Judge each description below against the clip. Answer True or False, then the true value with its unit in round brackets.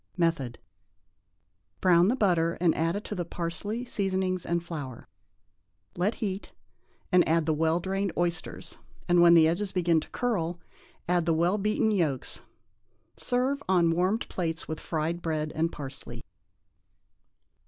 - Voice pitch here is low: False (175 Hz)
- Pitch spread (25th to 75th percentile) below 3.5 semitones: True (2.8 semitones)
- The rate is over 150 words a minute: False (145 wpm)